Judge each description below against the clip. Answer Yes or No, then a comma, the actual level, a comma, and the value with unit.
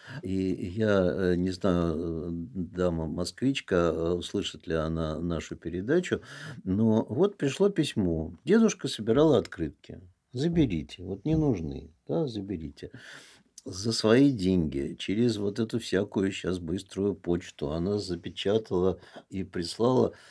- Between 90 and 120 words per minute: Yes, slow, 110 wpm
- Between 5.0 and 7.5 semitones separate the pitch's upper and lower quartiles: Yes, average, 5.3 semitones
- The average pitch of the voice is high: No, very low, 95 Hz